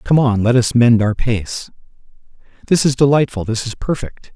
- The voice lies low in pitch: Yes, low, 120 Hz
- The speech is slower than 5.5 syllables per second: Yes, 4.9 syllables/s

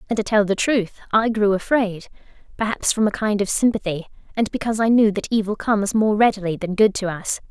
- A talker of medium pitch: No, high, 210 Hz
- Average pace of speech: No, fast, 215 wpm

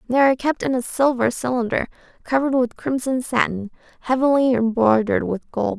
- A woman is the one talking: Yes, female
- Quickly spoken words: No, average, 155 wpm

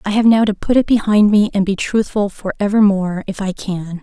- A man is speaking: No, female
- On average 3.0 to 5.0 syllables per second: No, 5.5 syllables/s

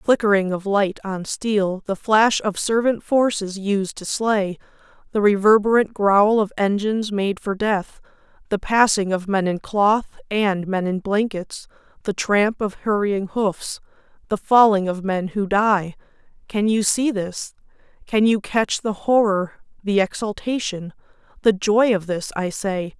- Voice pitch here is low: No, high, 205 Hz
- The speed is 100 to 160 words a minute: Yes, average, 150 wpm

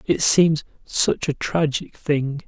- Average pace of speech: Yes, average, 145 wpm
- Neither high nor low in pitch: Yes, medium, 145 Hz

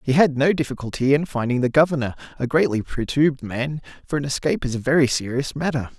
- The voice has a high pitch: No, low, 135 Hz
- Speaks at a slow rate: No, average, 200 wpm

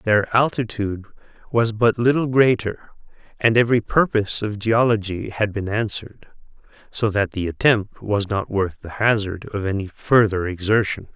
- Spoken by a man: Yes, male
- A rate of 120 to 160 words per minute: Yes, average, 145 wpm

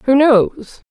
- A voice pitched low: No, very high, 255 Hz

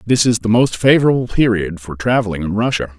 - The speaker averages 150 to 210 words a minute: Yes, average, 200 wpm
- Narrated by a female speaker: No, male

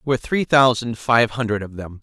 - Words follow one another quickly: Yes, fast, 235 wpm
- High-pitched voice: No, low, 115 Hz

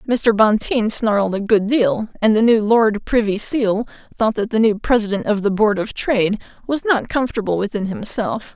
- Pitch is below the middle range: No, high, 215 Hz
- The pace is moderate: Yes, average, 190 wpm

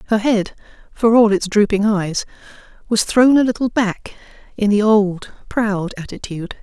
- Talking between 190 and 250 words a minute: No, average, 155 wpm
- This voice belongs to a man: No, female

